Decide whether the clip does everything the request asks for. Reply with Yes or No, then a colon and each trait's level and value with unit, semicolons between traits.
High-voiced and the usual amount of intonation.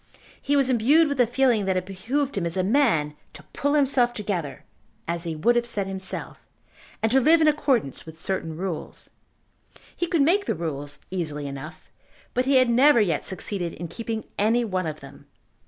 No: high, 210 Hz; wide, 7.8 semitones